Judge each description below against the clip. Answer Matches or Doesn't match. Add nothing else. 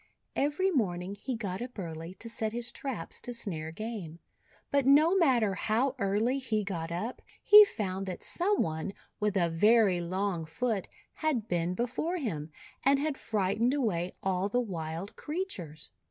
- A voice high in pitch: Matches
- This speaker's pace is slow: Doesn't match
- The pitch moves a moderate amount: Doesn't match